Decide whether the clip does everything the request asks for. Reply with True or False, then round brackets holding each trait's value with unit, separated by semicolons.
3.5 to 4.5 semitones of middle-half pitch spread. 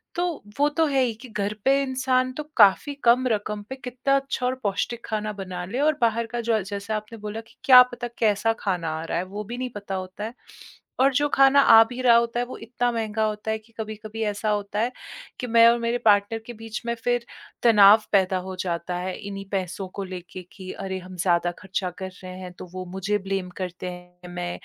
True (4.0 semitones)